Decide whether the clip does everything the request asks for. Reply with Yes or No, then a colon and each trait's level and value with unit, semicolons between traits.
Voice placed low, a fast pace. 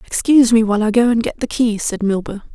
No: high, 225 Hz; fast, 260 wpm